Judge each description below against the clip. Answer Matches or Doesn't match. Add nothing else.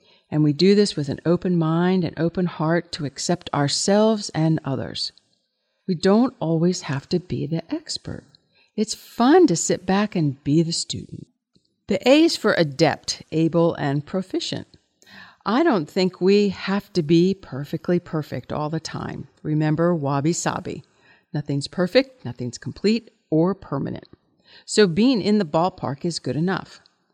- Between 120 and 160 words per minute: Matches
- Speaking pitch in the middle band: Matches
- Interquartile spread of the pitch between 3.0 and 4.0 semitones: Doesn't match